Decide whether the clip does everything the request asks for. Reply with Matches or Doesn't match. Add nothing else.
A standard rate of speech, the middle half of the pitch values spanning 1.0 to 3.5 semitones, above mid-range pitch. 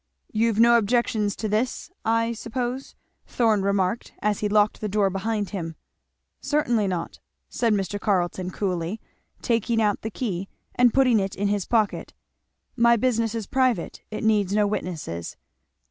Matches